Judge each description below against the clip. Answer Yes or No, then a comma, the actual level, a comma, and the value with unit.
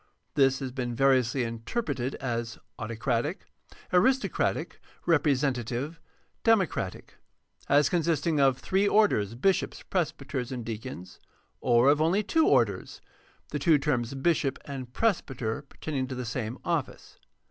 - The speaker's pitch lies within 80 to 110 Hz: No, low, 135 Hz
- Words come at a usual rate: No, slow, 125 wpm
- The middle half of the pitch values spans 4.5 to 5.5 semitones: Yes, average, 4.9 semitones